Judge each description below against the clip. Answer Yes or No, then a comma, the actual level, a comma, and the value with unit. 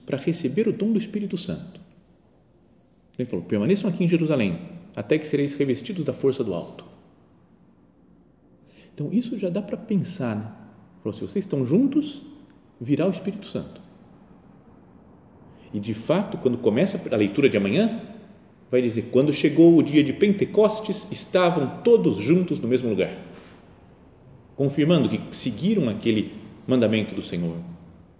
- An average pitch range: No, wide, 8.1 semitones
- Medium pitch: Yes, medium, 165 Hz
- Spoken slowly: No, average, 145 wpm